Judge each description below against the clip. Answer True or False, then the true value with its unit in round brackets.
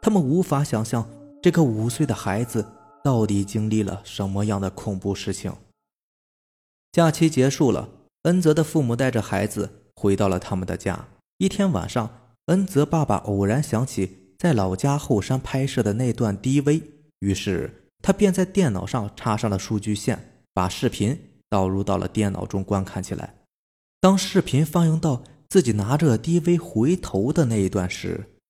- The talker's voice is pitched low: True (115 Hz)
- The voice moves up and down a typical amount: False (7.3 semitones)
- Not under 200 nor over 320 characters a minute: True (250 characters per minute)